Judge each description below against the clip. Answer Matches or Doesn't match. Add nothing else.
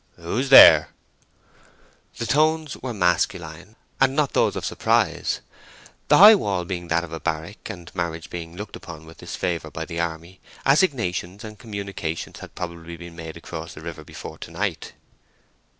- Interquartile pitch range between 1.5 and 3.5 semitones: Doesn't match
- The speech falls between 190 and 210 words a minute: Doesn't match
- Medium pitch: Doesn't match